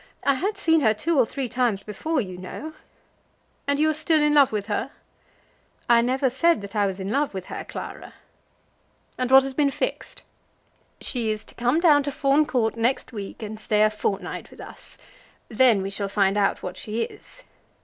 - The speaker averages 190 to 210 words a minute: Yes, average, 200 wpm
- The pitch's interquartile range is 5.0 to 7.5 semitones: Yes, wide, 5.4 semitones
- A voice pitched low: No, high, 240 Hz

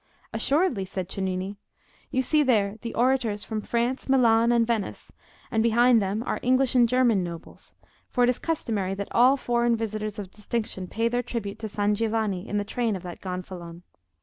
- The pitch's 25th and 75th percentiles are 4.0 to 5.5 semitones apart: No, average, 3.4 semitones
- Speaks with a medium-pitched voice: No, high, 225 Hz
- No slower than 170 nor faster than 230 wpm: Yes, average, 180 wpm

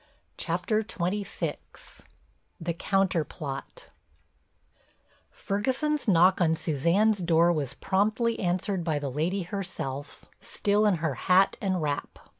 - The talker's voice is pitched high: No, medium, 180 Hz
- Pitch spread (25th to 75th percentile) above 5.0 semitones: No, average, 3.9 semitones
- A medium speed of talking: No, slow, 105 wpm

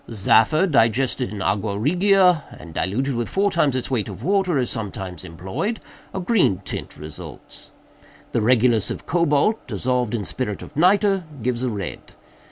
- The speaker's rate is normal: Yes, average, 160 wpm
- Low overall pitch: Yes, low, 125 Hz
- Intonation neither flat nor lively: No, wide, 8.7 semitones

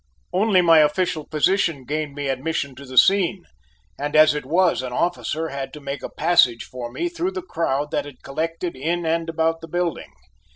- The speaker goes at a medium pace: Yes, average, 195 wpm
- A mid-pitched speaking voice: Yes, medium, 160 Hz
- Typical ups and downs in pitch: Yes, average, 3.7 semitones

